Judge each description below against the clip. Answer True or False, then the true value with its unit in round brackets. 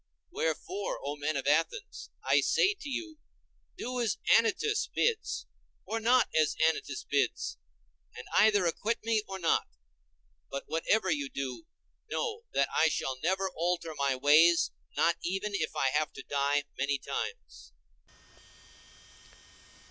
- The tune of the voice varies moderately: False (8.3 semitones)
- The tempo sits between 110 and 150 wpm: True (135 wpm)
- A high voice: False (175 Hz)